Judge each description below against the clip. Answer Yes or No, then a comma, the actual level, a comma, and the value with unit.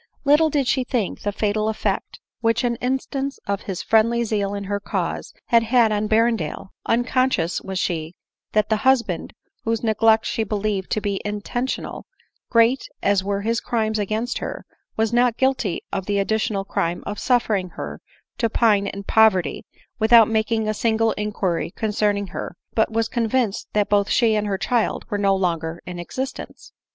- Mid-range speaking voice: No, high, 215 Hz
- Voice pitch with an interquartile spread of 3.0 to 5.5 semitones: No, narrow, 2.5 semitones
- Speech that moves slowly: No, average, 175 wpm